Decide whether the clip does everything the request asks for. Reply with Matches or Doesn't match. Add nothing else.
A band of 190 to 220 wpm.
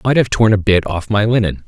Doesn't match